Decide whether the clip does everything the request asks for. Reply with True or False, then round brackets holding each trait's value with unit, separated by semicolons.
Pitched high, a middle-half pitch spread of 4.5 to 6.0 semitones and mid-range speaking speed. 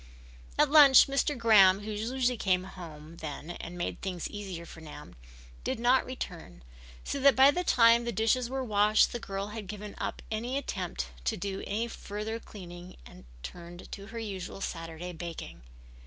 True (205 Hz; 5.1 semitones; 170 wpm)